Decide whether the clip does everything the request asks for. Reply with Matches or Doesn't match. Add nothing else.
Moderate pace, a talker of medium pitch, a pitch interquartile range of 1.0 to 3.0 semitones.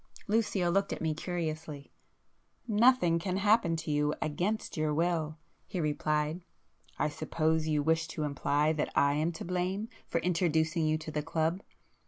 Matches